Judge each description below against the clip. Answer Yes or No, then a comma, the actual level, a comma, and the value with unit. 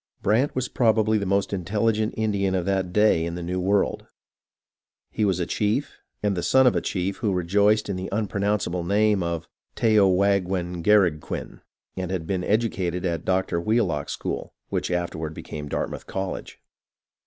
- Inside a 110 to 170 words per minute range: Yes, average, 165 wpm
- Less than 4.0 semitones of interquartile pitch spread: Yes, average, 3.0 semitones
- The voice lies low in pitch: Yes, very low, 95 Hz